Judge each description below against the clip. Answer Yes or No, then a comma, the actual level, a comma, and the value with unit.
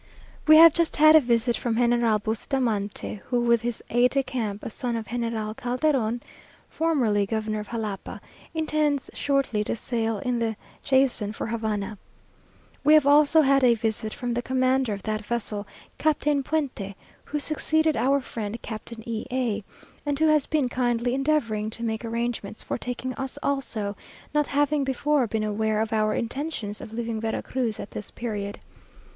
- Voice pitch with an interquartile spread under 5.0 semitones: Yes, average, 4.0 semitones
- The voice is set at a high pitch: Yes, high, 240 Hz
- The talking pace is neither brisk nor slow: Yes, average, 170 wpm